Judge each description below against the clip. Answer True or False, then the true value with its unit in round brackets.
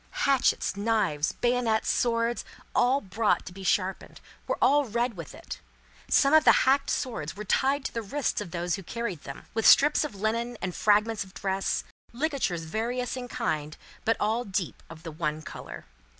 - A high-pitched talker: True (220 Hz)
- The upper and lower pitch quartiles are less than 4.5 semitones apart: False (5.1 semitones)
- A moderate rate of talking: True (180 wpm)